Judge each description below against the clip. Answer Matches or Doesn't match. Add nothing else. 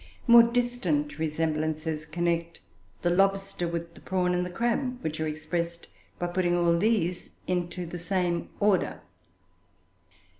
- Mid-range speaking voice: Matches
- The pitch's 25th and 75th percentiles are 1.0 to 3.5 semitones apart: Matches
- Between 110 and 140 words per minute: Matches